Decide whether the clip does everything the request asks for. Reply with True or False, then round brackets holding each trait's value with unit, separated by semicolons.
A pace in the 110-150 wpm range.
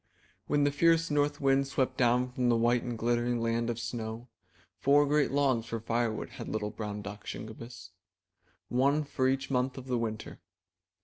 False (175 wpm)